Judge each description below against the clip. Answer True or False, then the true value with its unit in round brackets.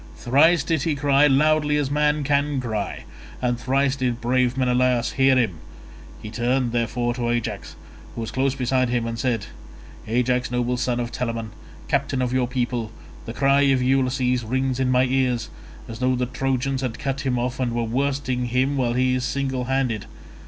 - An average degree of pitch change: False (1.9 semitones)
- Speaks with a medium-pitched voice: False (125 Hz)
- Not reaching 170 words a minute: False (185 wpm)